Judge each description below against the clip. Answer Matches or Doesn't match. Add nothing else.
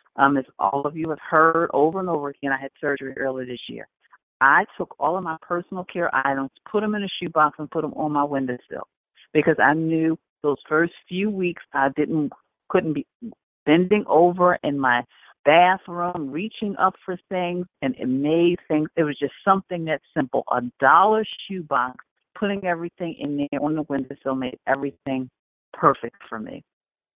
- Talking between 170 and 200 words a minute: Matches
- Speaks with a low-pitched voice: Doesn't match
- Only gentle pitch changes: Doesn't match